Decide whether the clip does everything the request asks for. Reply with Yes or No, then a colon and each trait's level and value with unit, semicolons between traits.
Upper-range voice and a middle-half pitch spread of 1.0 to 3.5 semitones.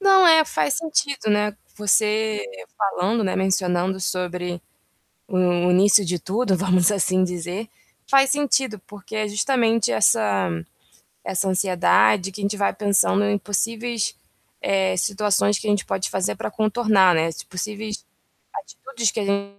Yes: high, 200 Hz; average, 2.9 semitones